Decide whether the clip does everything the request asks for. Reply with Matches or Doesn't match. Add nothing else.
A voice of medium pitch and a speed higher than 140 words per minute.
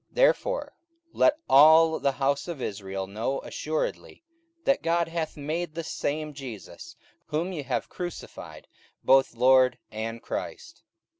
Doesn't match